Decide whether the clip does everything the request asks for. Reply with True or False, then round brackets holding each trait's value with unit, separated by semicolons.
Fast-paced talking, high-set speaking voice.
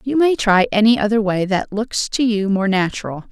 True (215 wpm; 210 Hz)